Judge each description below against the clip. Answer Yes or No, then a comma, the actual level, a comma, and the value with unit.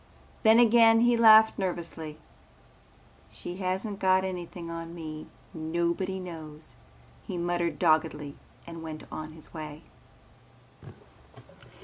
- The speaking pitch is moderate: Yes, medium, 170 Hz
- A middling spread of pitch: Yes, average, 3.1 semitones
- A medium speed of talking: No, slow, 105 wpm